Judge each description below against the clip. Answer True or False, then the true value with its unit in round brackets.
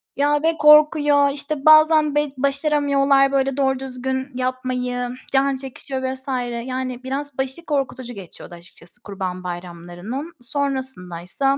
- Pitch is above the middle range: True (265 Hz)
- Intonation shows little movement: True (2.3 semitones)